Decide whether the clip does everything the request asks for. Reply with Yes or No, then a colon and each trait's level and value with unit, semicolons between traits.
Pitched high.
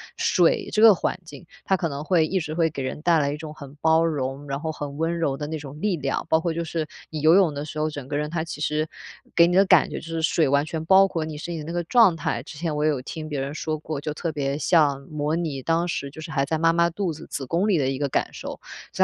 No: medium, 155 Hz